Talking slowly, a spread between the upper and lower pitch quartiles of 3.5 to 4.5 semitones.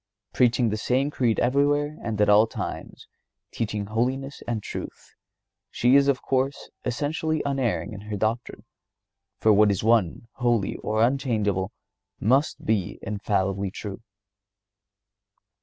Yes: slow, 125 wpm; average, 4.2 semitones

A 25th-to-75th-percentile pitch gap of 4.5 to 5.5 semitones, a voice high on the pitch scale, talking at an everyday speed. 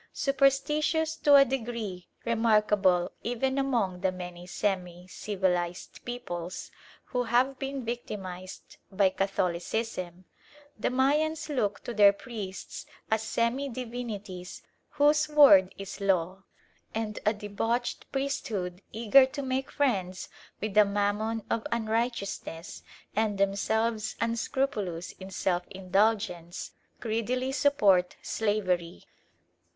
No: average, 4.8 semitones; high, 215 Hz; slow, 105 wpm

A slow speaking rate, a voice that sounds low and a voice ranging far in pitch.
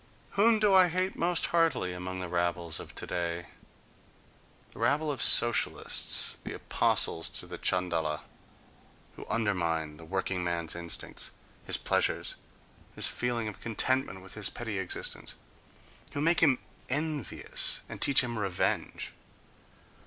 Yes: slow, 125 wpm; low, 100 Hz; wide, 8.6 semitones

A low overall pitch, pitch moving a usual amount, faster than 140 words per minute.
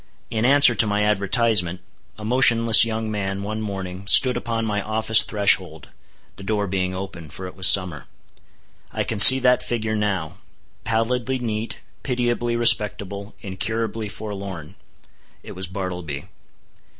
No: low, 105 Hz; average, 3.1 semitones; slow, 135 wpm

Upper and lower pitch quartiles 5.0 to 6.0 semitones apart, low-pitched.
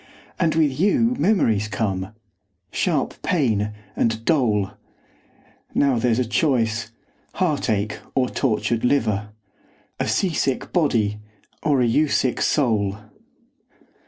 Yes: wide, 5.4 semitones; low, 120 Hz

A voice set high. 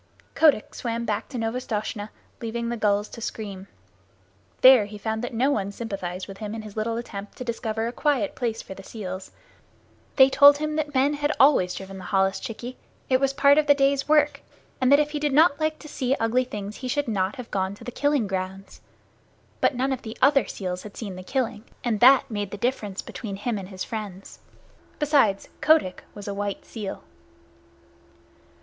Yes: high, 225 Hz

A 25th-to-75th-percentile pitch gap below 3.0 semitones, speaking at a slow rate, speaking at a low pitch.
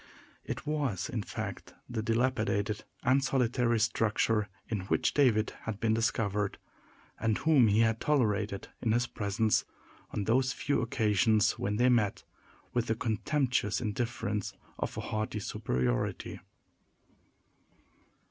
Yes: narrow, 2.6 semitones; slow, 125 wpm; low, 110 Hz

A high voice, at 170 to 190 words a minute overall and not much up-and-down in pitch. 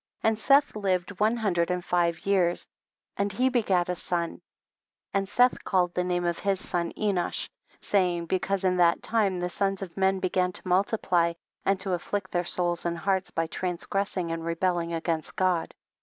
No: medium, 180 Hz; average, 180 wpm; narrow, 2.2 semitones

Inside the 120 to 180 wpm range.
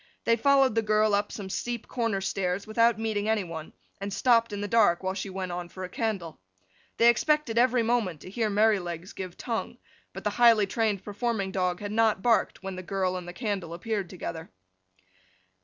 No: average, 195 wpm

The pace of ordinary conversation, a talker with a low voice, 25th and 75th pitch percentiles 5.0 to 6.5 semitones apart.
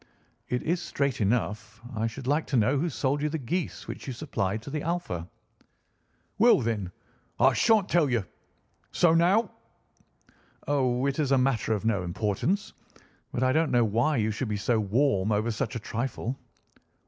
Yes: average, 175 wpm; low, 130 Hz; wide, 5.6 semitones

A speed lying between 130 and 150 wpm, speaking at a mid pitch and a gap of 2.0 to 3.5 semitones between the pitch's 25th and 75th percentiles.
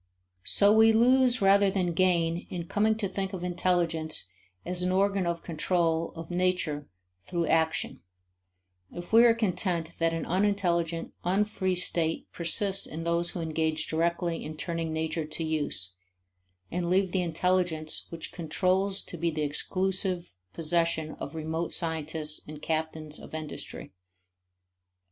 Yes: average, 140 wpm; medium, 170 Hz; narrow, 2.6 semitones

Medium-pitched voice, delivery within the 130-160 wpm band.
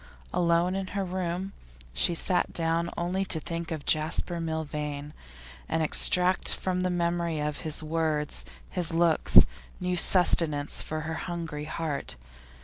Yes: medium, 165 Hz; average, 140 wpm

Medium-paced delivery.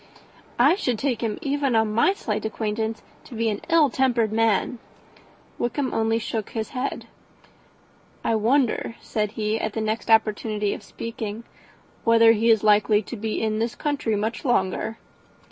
Yes: average, 160 wpm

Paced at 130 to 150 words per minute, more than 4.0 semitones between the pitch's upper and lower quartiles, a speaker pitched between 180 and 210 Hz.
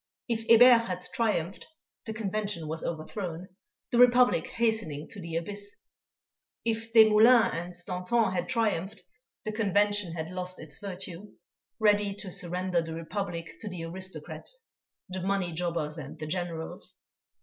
Yes: average, 140 wpm; average, 4.4 semitones; high, 190 Hz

